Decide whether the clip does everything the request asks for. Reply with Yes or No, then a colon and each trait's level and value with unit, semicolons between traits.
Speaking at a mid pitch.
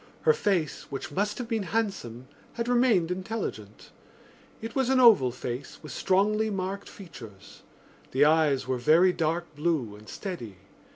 Yes: medium, 175 Hz